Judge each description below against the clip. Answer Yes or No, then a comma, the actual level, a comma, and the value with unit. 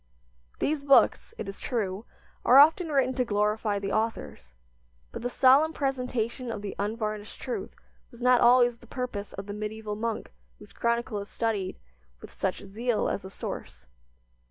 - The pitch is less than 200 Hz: No, high, 225 Hz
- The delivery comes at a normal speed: Yes, average, 160 wpm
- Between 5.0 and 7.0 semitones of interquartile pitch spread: No, average, 3.5 semitones